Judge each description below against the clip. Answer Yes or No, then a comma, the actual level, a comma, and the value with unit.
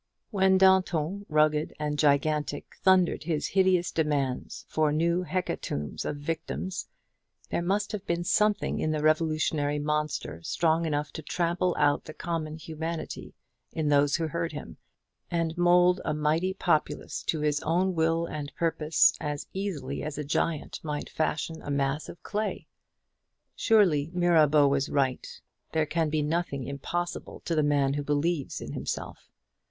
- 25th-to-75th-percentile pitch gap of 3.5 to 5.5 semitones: No, average, 2.7 semitones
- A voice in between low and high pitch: Yes, medium, 155 Hz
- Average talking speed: Yes, average, 150 wpm